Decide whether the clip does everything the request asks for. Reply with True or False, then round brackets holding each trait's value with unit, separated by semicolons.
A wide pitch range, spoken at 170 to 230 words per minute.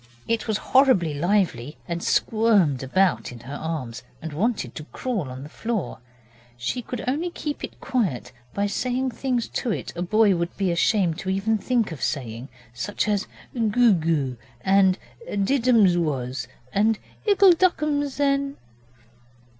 False (7.7 semitones; 155 wpm)